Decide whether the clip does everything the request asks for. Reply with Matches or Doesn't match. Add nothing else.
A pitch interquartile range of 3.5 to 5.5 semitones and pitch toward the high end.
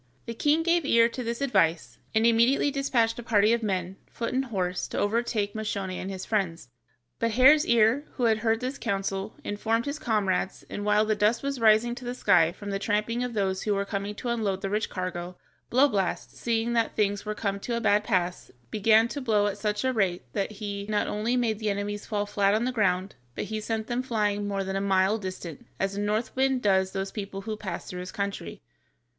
Doesn't match